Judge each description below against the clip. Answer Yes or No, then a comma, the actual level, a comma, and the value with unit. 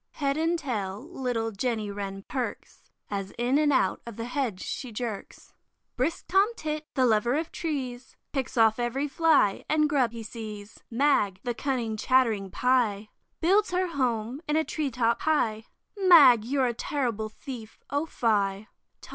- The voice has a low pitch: No, high, 245 Hz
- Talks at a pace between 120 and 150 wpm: No, average, 160 wpm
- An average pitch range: Yes, average, 4.8 semitones